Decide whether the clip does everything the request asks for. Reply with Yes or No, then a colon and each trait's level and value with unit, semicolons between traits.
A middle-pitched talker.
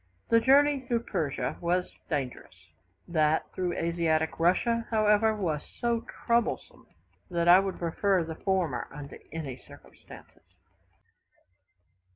Yes: medium, 175 Hz